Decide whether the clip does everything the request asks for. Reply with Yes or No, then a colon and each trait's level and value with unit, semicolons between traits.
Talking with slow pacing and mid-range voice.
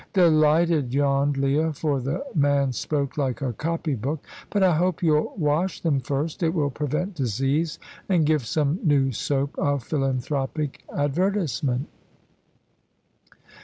Yes: slow, 130 wpm; medium, 145 Hz